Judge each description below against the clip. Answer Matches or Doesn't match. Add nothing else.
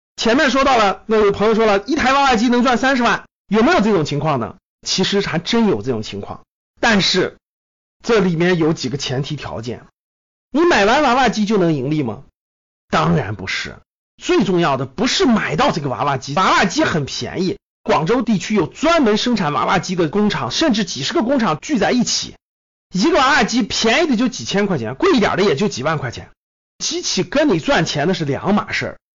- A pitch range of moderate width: Doesn't match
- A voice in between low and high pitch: Doesn't match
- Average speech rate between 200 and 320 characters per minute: Matches